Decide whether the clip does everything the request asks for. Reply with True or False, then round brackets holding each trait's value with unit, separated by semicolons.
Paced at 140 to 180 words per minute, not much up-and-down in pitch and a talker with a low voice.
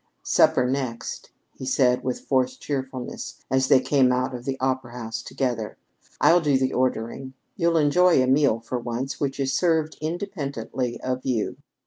True (160 wpm; 2.0 semitones; 130 Hz)